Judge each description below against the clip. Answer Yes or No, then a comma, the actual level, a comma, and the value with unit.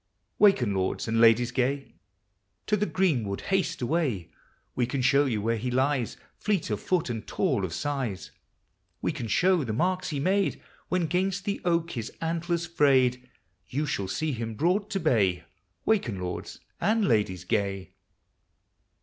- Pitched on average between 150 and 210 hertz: No, low, 135 Hz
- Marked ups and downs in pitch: Yes, wide, 7.6 semitones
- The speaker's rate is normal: Yes, average, 160 wpm